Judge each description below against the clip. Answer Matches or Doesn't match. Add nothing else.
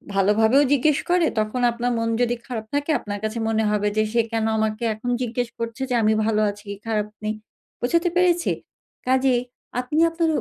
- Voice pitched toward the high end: Matches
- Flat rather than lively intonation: Doesn't match